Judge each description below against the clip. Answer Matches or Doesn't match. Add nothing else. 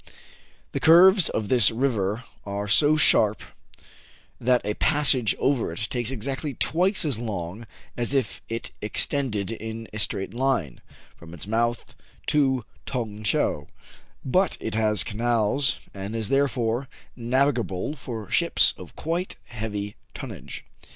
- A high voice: Doesn't match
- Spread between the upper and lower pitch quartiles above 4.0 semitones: Matches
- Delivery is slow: Matches